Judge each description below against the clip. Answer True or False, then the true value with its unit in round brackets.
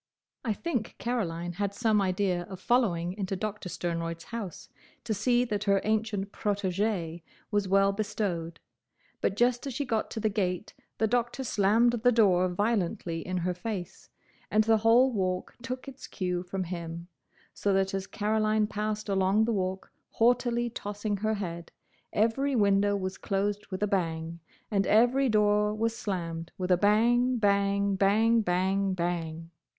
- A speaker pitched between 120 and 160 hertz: False (205 Hz)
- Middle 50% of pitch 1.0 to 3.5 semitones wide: True (3.2 semitones)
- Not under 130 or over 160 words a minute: True (155 wpm)